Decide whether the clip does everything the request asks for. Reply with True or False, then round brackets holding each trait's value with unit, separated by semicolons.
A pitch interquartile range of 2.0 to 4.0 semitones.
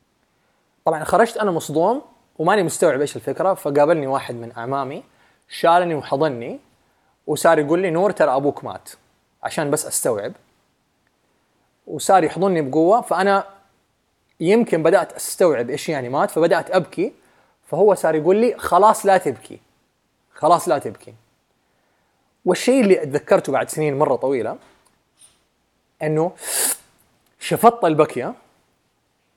False (4.9 semitones)